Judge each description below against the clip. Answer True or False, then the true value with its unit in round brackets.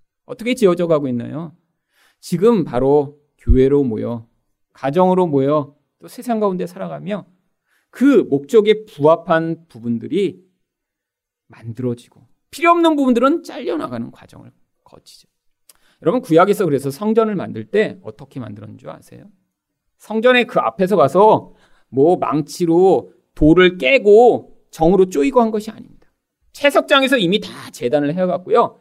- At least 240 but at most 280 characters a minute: False (300 characters per minute)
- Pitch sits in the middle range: True (175 Hz)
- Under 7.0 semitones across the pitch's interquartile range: False (7.6 semitones)